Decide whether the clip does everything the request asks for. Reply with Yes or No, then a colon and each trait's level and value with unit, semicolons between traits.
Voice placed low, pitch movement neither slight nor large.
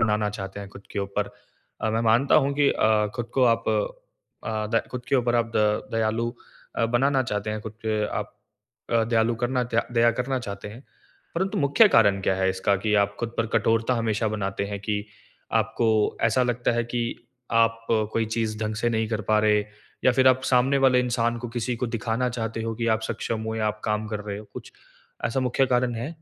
No: low, 115 Hz; narrow, 2.3 semitones